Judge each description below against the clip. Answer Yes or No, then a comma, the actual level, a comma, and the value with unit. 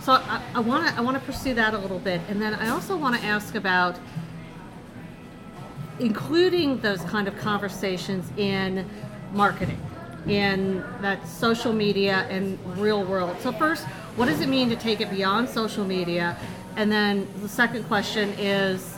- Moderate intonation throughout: Yes, average, 3.2 semitones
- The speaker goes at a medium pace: Yes, average, 160 wpm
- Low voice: No, high, 205 Hz